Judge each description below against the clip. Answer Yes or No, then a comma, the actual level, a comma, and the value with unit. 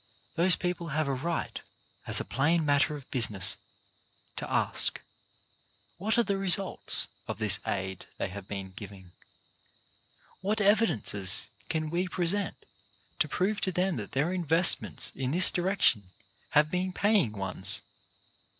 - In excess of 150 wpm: No, average, 140 wpm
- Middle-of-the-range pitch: Yes, medium, 160 Hz